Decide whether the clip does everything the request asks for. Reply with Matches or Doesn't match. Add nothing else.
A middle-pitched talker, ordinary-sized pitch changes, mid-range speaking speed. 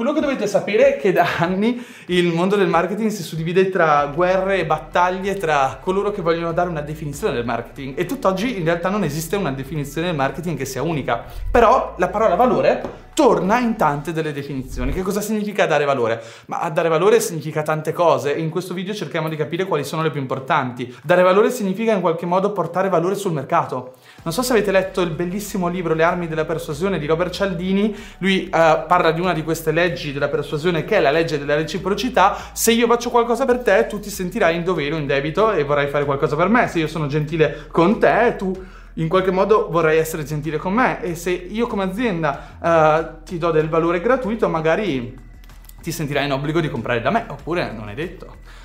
Doesn't match